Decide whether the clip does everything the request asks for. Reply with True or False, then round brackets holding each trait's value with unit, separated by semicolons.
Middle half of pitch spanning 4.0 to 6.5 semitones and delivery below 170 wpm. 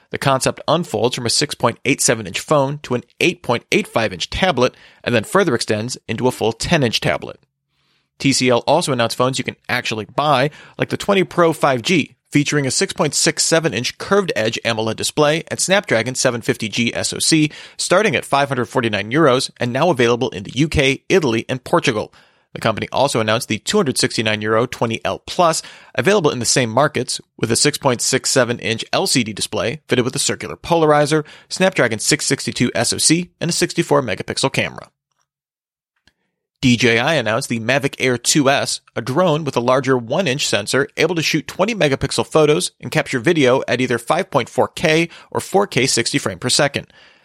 True (4.6 semitones; 160 wpm)